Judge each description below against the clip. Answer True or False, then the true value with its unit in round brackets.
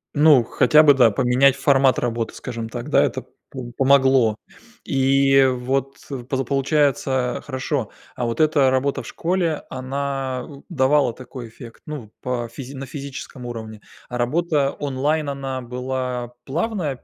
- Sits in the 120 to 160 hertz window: True (135 Hz)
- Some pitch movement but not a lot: False (2.3 semitones)